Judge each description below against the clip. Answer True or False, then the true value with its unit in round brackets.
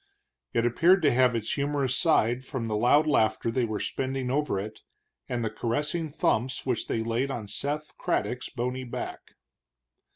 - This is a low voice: True (125 Hz)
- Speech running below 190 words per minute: True (165 wpm)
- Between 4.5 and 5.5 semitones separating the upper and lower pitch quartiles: False (3.5 semitones)